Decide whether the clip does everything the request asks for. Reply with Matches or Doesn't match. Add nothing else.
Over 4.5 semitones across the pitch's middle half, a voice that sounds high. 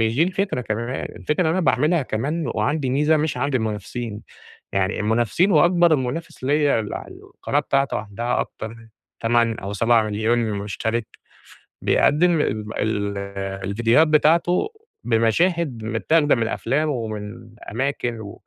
Doesn't match